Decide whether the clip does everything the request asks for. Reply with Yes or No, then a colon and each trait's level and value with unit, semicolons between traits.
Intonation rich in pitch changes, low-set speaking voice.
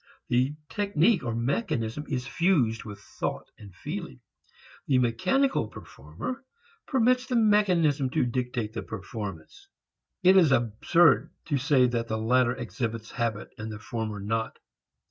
Yes: wide, 7.0 semitones; low, 125 Hz